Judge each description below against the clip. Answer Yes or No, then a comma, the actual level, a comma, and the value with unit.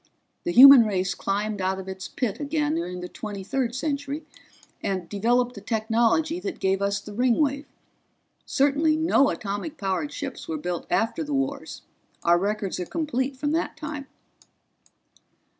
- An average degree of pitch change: No, wide, 6.6 semitones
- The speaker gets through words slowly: No, average, 155 wpm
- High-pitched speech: Yes, high, 245 Hz